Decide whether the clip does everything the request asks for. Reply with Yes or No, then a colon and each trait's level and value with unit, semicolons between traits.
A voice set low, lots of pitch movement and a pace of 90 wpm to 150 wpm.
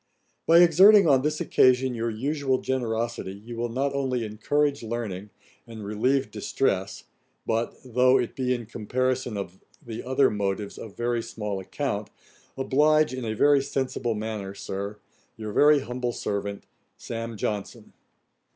No: low, 120 Hz; average, 3.7 semitones; average, 140 wpm